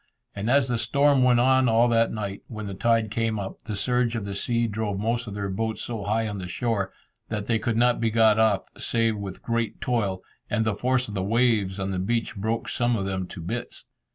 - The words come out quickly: Yes, fast, 235 wpm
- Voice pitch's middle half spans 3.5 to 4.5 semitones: No, average, 2.7 semitones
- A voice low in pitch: Yes, low, 110 Hz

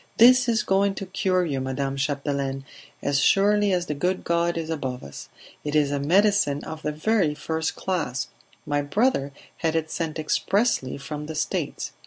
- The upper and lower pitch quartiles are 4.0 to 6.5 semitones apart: Yes, average, 5.0 semitones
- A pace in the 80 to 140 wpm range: No, average, 175 wpm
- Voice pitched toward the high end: No, medium, 160 Hz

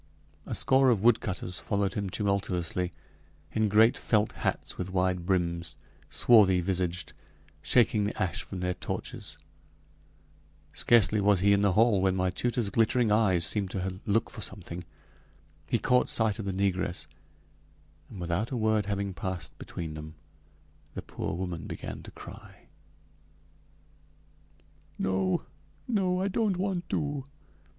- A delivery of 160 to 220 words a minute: No, average, 140 wpm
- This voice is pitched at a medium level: No, low, 100 Hz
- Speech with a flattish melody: No, average, 3.5 semitones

